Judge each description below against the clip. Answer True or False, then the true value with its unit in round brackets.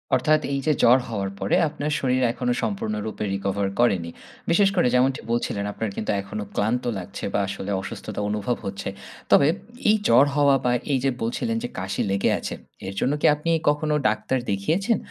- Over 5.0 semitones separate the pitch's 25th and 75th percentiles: True (5.6 semitones)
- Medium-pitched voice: False (115 Hz)